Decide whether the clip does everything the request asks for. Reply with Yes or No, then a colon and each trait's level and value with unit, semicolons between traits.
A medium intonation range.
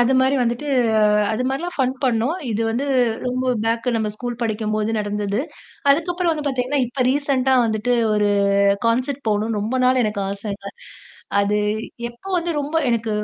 Yes: average, 3.8 semitones